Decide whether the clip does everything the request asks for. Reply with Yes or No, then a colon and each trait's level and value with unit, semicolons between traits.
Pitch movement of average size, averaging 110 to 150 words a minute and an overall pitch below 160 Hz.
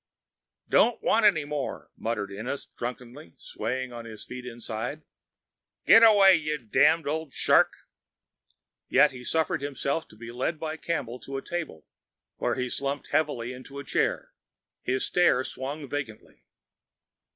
Yes: average, 4.3 semitones; average, 140 wpm; low, 135 Hz